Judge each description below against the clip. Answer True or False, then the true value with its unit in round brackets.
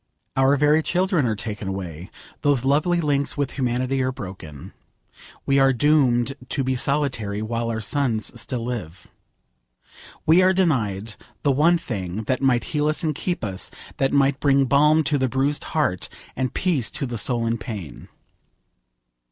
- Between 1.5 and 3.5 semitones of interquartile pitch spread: False (4.6 semitones)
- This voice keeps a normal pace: True (160 wpm)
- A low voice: True (130 Hz)